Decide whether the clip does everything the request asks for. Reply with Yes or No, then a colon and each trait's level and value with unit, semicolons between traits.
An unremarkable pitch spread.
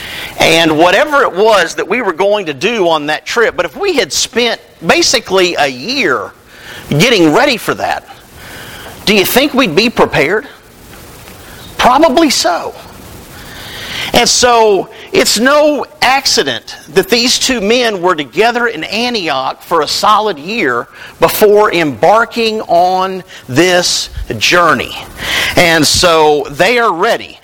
No: wide, 6.6 semitones